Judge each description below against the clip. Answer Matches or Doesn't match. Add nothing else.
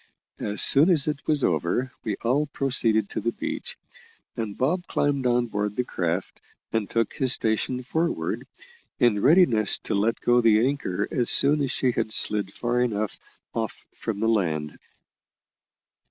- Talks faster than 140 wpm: Matches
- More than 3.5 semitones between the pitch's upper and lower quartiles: Matches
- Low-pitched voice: Matches